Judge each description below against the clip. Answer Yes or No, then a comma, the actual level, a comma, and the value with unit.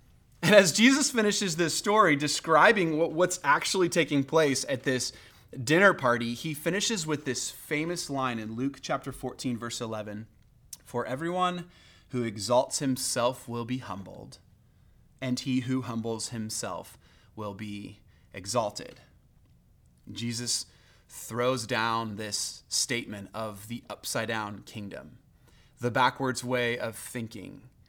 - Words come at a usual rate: No, slow, 125 wpm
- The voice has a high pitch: No, low, 125 Hz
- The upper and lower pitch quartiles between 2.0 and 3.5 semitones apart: No, average, 5.3 semitones